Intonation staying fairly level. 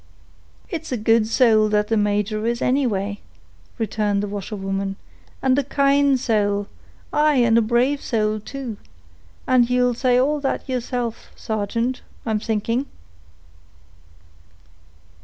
No: average, 3.4 semitones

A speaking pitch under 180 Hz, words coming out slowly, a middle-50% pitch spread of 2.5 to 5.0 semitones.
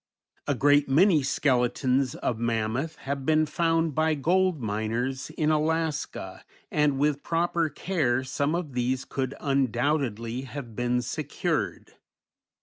Yes: medium, 140 Hz; slow, 125 wpm; average, 4.1 semitones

